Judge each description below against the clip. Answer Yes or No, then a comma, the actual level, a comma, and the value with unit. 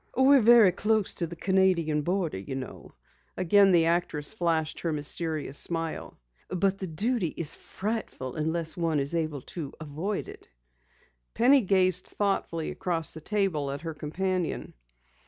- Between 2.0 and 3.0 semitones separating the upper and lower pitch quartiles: No, average, 3.8 semitones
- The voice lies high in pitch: No, medium, 170 Hz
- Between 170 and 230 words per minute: No, average, 145 wpm